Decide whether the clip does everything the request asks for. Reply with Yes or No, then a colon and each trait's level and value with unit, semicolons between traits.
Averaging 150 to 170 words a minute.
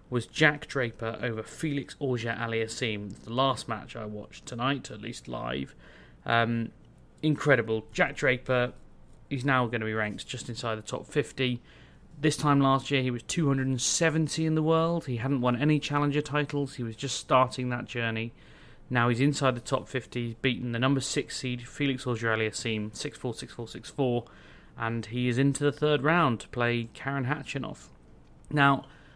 No: average, 180 wpm